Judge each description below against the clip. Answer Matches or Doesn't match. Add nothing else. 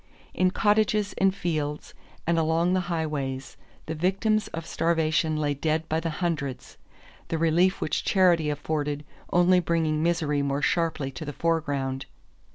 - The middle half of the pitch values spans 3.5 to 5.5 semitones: Doesn't match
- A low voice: Doesn't match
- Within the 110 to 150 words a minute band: Matches